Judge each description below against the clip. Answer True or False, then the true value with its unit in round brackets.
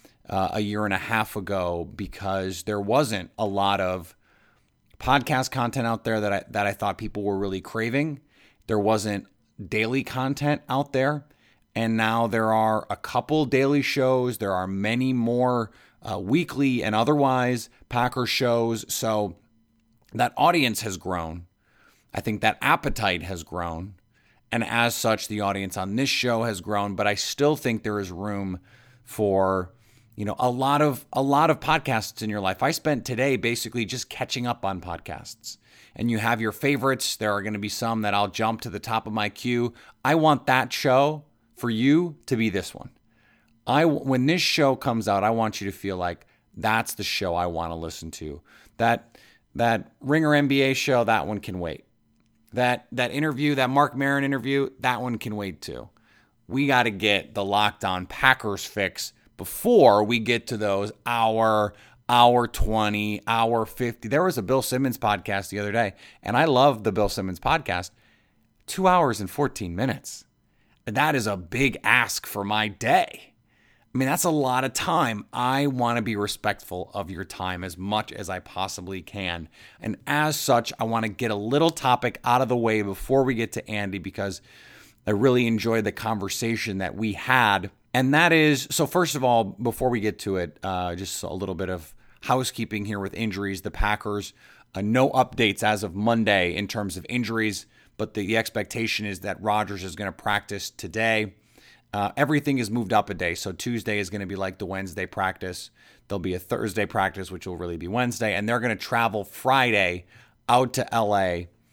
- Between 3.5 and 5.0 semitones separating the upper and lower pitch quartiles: True (3.9 semitones)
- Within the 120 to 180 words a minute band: False (190 wpm)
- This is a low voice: True (110 Hz)